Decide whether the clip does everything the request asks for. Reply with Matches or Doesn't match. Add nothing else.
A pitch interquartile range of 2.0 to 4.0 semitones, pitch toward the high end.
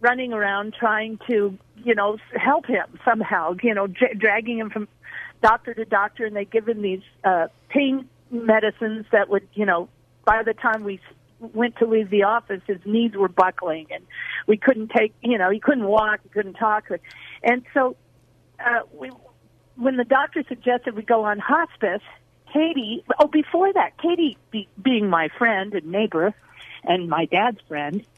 Matches